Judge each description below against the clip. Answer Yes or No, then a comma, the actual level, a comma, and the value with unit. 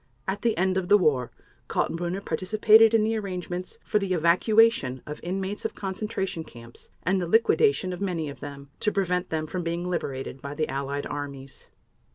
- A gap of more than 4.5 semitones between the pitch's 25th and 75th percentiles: Yes, average, 4.9 semitones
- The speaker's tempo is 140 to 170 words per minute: No, average, 180 wpm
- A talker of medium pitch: Yes, medium, 180 Hz